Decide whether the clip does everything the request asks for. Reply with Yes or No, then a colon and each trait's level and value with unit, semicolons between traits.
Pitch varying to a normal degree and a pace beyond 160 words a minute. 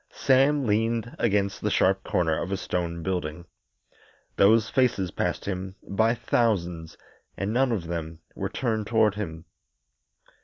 No: average, 4.6 semitones; average, 140 wpm